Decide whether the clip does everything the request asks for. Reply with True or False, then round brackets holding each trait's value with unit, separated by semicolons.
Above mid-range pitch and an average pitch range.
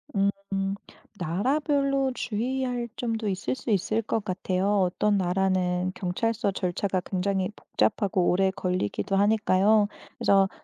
True (200 Hz; 3.3 semitones)